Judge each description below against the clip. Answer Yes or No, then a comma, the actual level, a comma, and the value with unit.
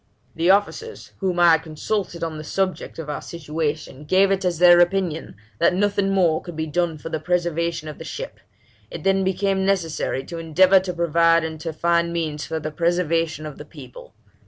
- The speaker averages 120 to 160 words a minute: No, average, 195 wpm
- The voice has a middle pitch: Yes, medium, 170 Hz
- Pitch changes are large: No, average, 2.7 semitones